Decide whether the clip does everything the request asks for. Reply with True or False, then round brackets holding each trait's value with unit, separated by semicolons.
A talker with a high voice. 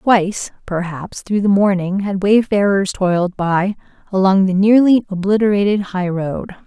True (195 Hz)